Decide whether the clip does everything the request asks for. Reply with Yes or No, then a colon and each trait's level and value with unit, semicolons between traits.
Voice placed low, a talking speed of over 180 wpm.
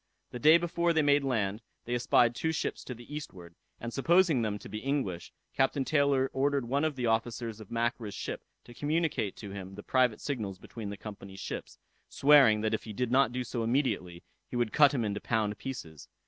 Yes: low, 120 Hz; fast, 205 wpm